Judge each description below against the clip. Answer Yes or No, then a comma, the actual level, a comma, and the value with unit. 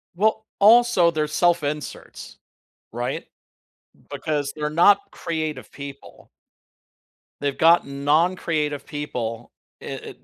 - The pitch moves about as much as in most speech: Yes, average, 3.3 semitones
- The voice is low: No, medium, 150 Hz